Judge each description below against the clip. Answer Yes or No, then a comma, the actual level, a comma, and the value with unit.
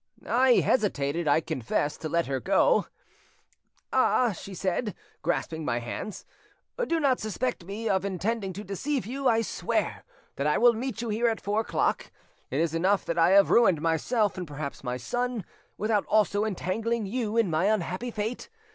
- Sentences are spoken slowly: No, average, 175 wpm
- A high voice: Yes, high, 200 Hz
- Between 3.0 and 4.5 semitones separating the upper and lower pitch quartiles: No, wide, 5.6 semitones